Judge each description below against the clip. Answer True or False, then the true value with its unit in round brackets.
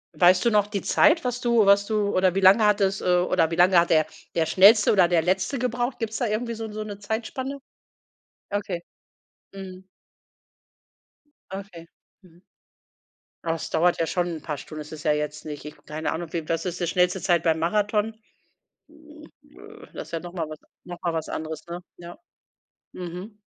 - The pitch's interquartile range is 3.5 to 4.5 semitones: True (4.0 semitones)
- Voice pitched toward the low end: False (185 Hz)